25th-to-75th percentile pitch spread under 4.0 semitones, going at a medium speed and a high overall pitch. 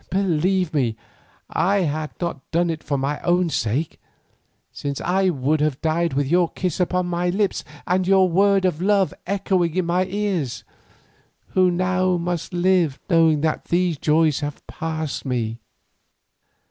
No: average, 3.3 semitones; average, 155 wpm; medium, 170 Hz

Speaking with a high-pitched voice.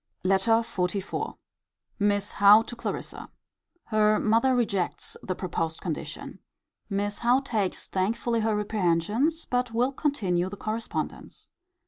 Yes: high, 210 Hz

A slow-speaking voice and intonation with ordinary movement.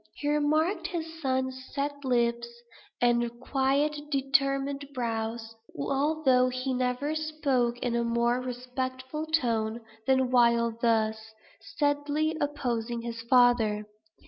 Yes: slow, 110 wpm; average, 3.4 semitones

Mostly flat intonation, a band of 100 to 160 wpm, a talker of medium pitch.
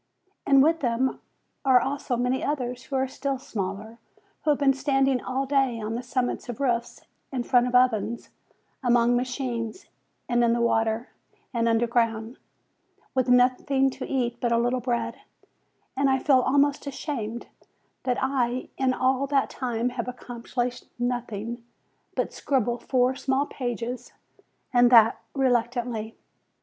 No: narrow, 2.1 semitones; average, 145 wpm; very high, 250 Hz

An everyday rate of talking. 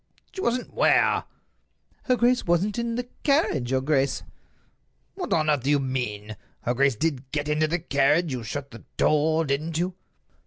Yes: average, 170 wpm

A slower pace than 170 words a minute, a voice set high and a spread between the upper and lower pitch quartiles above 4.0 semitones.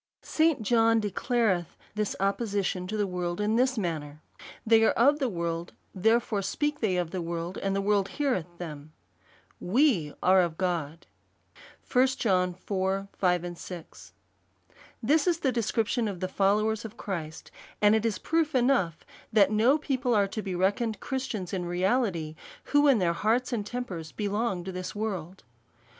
Yes: average, 160 wpm; high, 200 Hz; average, 4.6 semitones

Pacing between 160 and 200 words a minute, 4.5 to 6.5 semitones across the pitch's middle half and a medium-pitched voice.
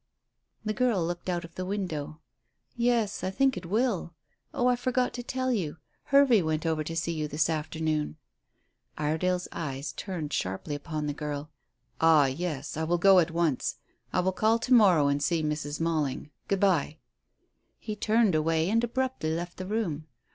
Yes: average, 175 wpm; average, 5.3 semitones; medium, 170 Hz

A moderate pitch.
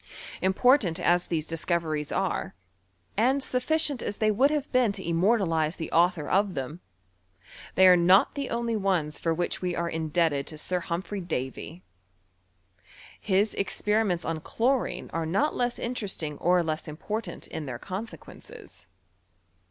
Yes: medium, 180 Hz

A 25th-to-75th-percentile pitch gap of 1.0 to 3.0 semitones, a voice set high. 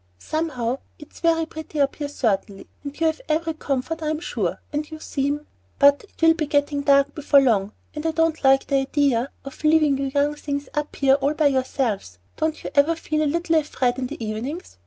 Yes: narrow, 2.6 semitones; very high, 285 Hz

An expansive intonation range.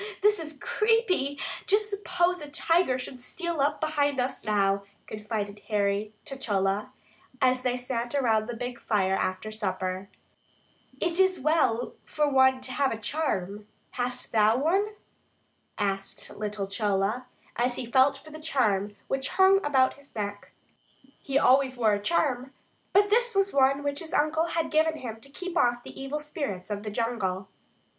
Yes: wide, 6.3 semitones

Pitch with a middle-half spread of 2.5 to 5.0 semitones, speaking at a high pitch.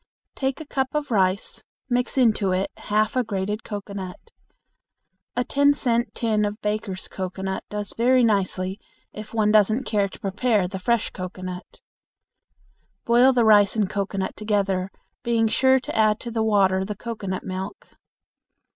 Yes: average, 3.4 semitones; high, 210 Hz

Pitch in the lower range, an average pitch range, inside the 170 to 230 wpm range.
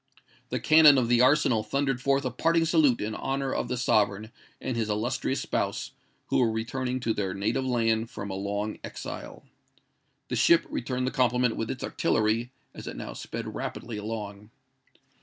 Yes: low, 120 Hz; average, 3.4 semitones; average, 175 wpm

